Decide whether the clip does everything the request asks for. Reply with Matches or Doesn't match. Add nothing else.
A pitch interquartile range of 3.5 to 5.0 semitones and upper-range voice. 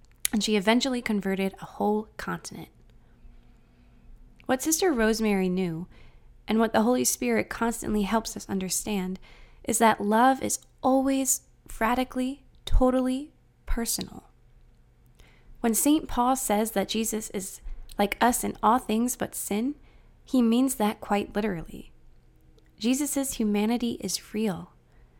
Matches